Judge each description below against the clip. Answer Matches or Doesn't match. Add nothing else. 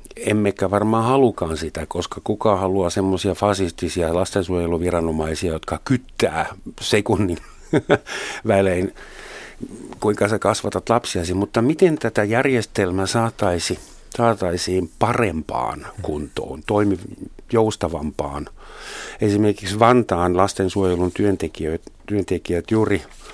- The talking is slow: Matches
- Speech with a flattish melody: Doesn't match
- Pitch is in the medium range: Doesn't match